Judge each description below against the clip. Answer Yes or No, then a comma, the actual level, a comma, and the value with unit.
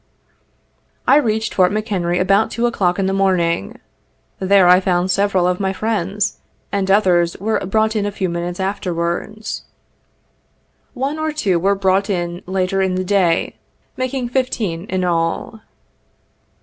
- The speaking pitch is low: No, high, 195 Hz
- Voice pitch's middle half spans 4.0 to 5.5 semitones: No, average, 3.1 semitones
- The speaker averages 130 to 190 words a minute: Yes, average, 145 wpm